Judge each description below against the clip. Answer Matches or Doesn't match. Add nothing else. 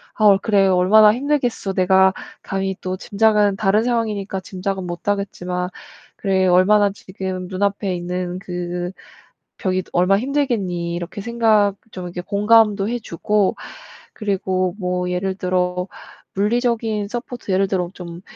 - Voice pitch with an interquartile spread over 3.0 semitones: Doesn't match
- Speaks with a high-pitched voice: Matches